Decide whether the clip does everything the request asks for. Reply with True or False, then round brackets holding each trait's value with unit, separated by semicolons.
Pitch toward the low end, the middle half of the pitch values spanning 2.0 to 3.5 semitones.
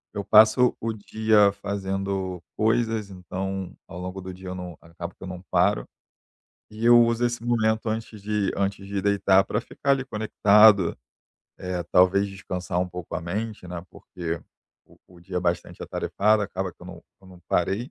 True (95 Hz; 3.1 semitones)